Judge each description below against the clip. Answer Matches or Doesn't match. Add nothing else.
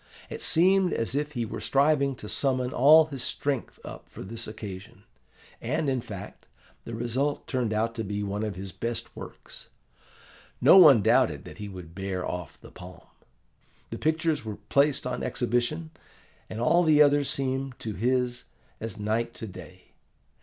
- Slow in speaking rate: Doesn't match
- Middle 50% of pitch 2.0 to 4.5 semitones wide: Doesn't match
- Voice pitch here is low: Matches